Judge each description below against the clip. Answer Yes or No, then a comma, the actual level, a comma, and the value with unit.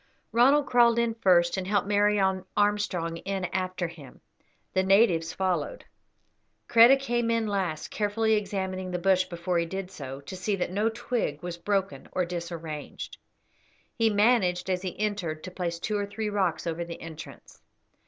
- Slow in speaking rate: No, average, 165 wpm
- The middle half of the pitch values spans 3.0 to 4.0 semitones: Yes, average, 3.4 semitones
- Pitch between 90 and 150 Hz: No, high, 190 Hz